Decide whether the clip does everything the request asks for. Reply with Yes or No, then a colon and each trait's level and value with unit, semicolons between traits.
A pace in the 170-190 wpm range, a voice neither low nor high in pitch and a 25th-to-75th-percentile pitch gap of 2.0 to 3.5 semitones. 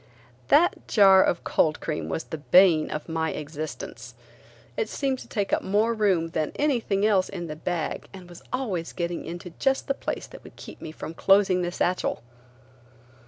No: average, 180 wpm; medium, 180 Hz; average, 4.1 semitones